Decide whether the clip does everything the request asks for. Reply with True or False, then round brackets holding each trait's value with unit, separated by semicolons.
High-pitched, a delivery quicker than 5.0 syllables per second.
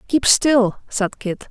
False (230 Hz; 3.2 syllables/s)